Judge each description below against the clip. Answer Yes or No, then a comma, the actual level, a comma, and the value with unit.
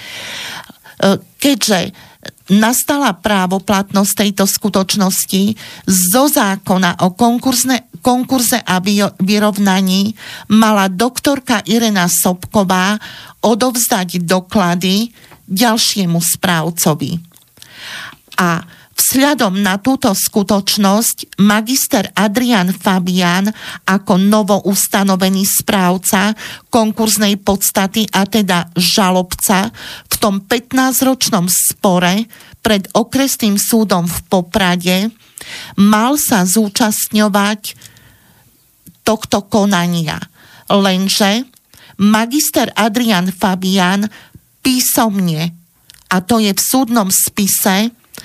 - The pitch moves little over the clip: No, average, 3.3 semitones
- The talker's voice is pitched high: Yes, high, 205 Hz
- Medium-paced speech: No, slow, 75 wpm